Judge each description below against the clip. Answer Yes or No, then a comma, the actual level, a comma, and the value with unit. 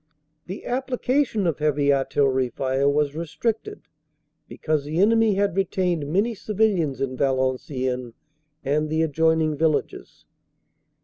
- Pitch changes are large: Yes, wide, 5.9 semitones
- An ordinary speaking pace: No, slow, 115 wpm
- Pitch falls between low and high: Yes, medium, 155 Hz